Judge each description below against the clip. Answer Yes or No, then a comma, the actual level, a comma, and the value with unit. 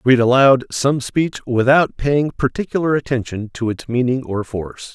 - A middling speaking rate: Yes, average, 160 wpm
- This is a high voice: No, low, 130 Hz